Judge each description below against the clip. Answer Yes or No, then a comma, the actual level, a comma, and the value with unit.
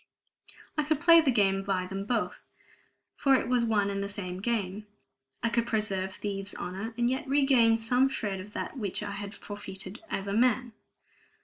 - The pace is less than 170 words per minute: No, average, 185 wpm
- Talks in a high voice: Yes, high, 210 Hz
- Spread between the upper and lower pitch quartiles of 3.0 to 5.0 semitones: Yes, average, 3.6 semitones